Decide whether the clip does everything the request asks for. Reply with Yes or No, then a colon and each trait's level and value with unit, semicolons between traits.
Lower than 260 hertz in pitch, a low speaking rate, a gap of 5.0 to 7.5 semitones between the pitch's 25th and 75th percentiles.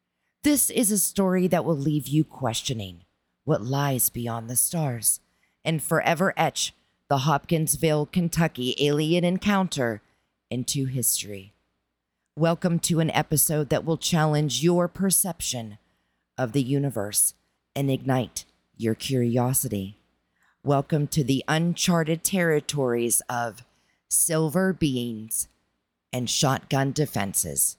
Yes: medium, 140 Hz; slow, 110 wpm; wide, 5.6 semitones